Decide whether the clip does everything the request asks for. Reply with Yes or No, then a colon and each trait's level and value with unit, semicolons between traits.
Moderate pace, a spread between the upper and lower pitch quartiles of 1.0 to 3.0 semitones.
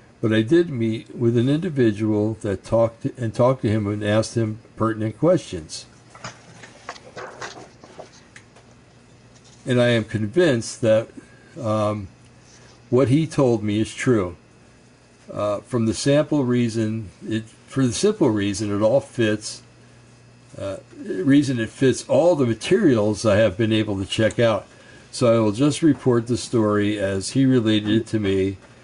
Yes: average, 150 wpm; average, 2.7 semitones